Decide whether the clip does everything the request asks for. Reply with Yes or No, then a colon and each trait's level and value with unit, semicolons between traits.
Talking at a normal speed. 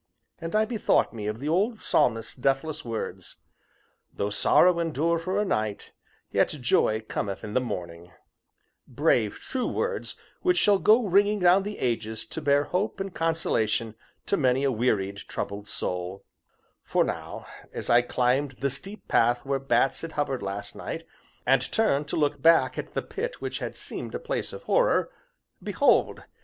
Yes: average, 165 wpm